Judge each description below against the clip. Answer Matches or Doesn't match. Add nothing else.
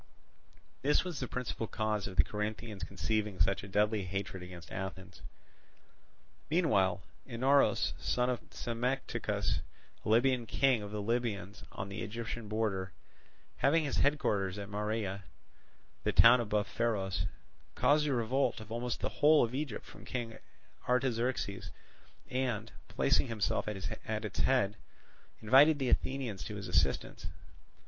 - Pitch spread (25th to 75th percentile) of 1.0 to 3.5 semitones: Doesn't match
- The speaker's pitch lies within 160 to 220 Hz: Doesn't match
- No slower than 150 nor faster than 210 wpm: Doesn't match